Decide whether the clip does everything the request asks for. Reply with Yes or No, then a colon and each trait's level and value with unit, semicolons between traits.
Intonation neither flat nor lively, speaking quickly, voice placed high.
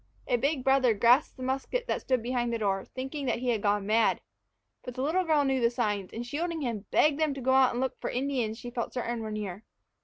Yes: average, 3.1 semitones; fast, 250 wpm; very high, 250 Hz